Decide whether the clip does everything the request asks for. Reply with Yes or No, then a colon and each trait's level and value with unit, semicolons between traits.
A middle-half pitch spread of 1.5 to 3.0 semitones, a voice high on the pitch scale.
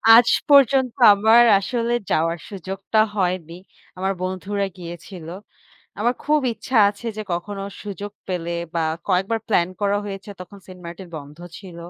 No: average, 3.6 semitones; high, 195 Hz